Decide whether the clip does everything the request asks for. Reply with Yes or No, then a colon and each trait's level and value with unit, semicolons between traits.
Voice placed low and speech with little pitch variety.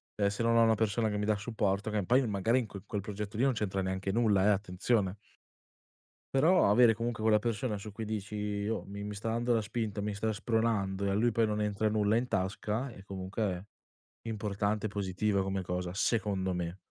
Yes: low, 105 Hz; narrow, 2.2 semitones